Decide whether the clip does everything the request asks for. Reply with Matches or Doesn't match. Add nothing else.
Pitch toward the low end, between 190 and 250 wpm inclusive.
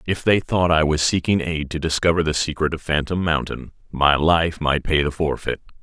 Matches